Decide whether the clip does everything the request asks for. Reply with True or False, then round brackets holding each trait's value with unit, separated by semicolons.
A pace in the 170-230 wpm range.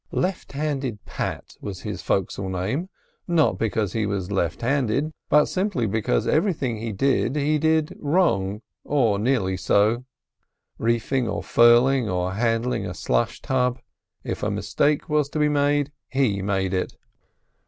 False (140 wpm)